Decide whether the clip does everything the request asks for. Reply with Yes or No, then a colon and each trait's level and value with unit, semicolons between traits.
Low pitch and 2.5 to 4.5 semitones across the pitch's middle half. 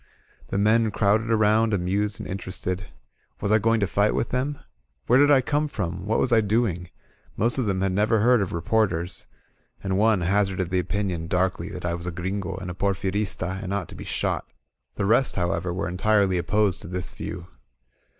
Yes: low, 100 Hz; average, 3.1 semitones